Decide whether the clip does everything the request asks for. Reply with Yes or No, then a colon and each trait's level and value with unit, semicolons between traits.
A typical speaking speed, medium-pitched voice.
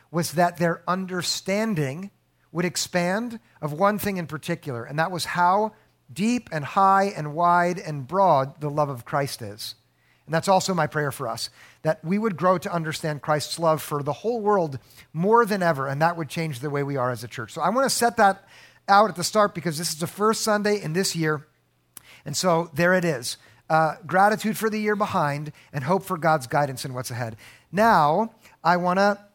No: fast, 210 wpm; medium, 170 Hz